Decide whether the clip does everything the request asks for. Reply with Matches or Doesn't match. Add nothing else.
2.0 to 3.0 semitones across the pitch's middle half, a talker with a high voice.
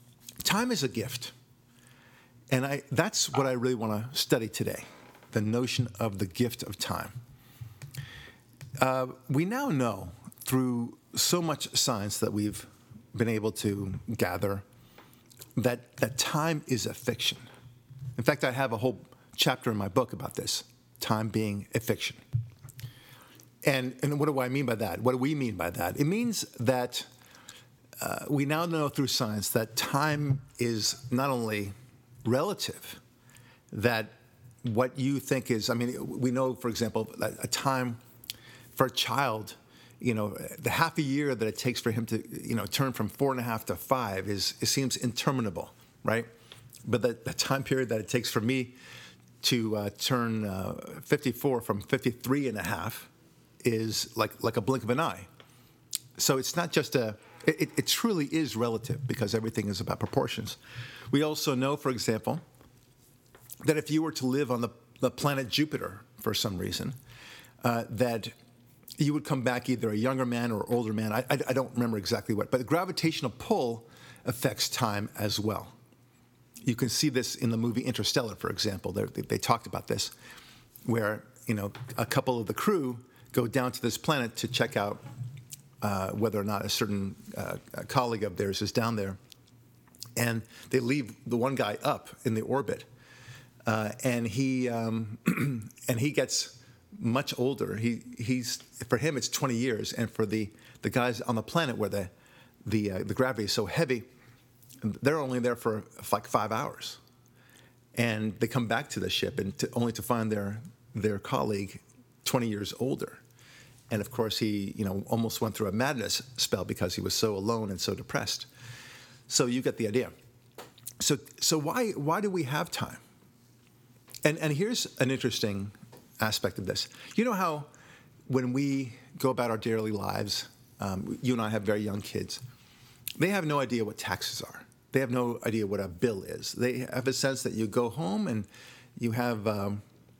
Doesn't match